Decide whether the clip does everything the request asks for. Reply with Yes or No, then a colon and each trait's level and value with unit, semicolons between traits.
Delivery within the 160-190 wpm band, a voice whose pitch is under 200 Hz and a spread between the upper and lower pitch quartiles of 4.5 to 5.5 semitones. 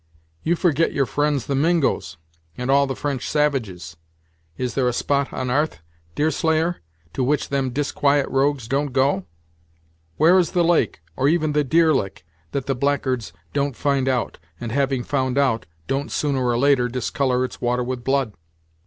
No: average, 170 wpm; low, 135 Hz; narrow, 2.6 semitones